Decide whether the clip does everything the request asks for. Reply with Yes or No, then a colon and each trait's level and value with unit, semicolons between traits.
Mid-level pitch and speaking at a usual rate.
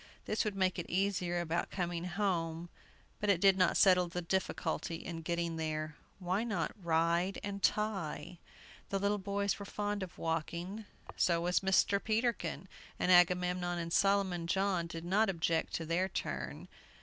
Yes: medium, 180 Hz; average, 160 wpm